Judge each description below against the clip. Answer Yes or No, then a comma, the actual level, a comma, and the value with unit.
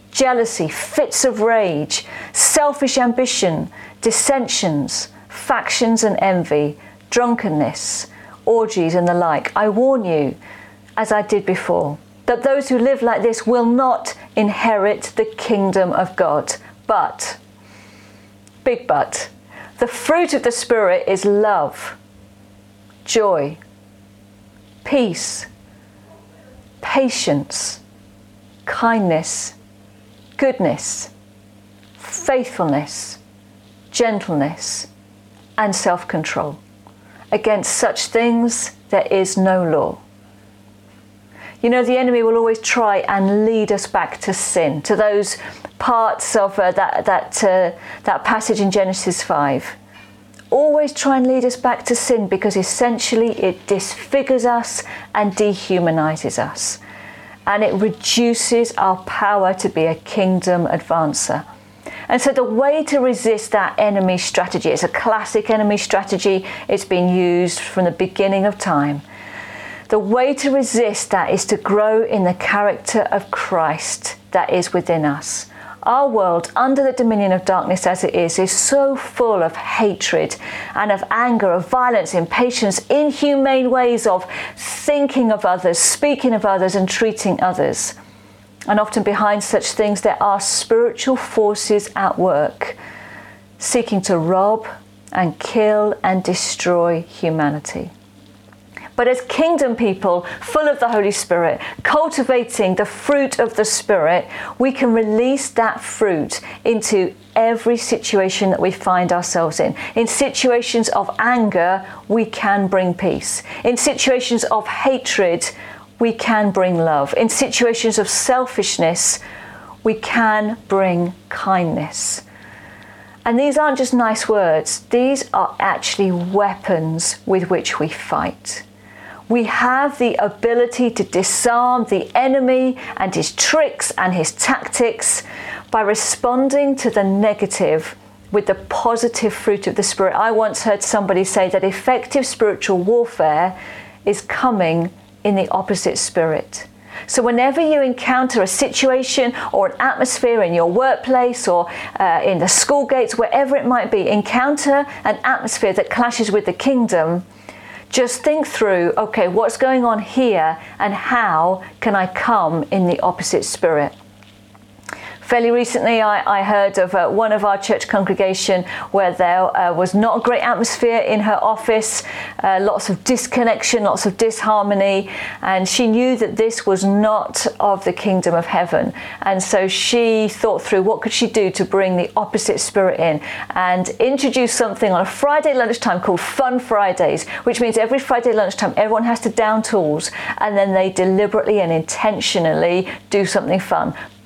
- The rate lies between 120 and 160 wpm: Yes, slow, 135 wpm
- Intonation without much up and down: No, average, 5.2 semitones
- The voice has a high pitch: Yes, high, 205 Hz